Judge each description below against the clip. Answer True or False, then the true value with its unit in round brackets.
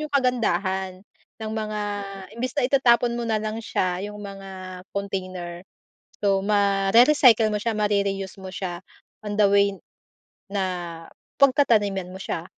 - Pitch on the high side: True (205 Hz)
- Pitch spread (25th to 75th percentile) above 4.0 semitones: False (2.8 semitones)